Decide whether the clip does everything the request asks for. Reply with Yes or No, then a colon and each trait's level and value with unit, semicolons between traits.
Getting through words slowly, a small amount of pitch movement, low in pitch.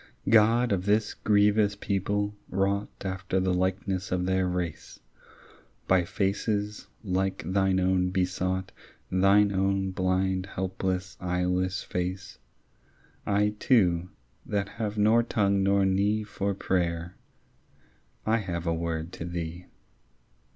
Yes: slow, 115 wpm; narrow, 1.8 semitones; very low, 95 Hz